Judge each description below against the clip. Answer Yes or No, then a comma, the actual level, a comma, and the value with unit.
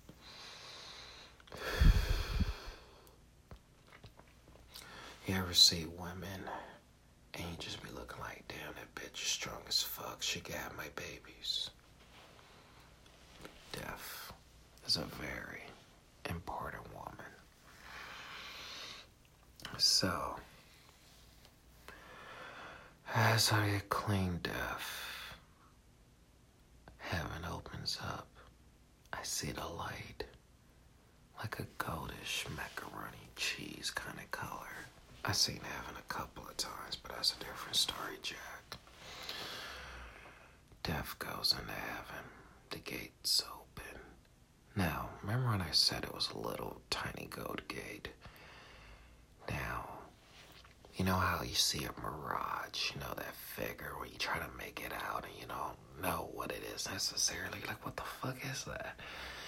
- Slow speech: Yes, slow, 115 wpm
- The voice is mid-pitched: No, very low, 85 Hz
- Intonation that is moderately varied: No, wide, 7.0 semitones